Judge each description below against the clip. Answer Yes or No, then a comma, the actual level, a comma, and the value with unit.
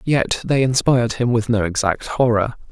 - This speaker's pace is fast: No, average, 175 wpm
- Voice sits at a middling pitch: No, low, 120 Hz